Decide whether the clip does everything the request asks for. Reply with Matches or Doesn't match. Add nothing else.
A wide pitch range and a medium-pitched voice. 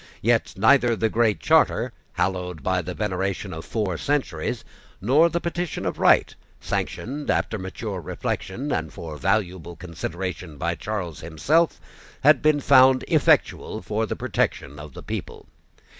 Doesn't match